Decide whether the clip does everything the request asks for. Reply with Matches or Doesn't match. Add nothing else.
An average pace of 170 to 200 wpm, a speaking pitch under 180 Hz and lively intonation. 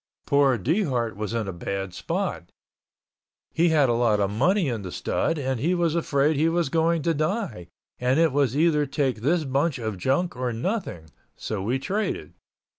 Matches